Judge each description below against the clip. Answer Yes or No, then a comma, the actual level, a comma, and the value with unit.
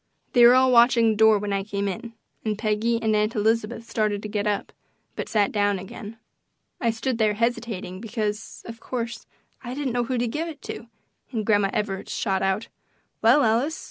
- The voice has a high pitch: Yes, high, 220 Hz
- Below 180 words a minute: No, average, 195 wpm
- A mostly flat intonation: Yes, narrow, 2.3 semitones